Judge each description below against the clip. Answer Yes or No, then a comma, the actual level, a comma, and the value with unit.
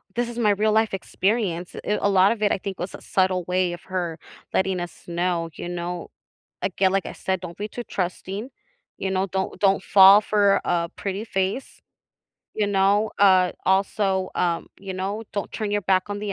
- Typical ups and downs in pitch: No, narrow, 2.1 semitones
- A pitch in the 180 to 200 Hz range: Yes, high, 190 Hz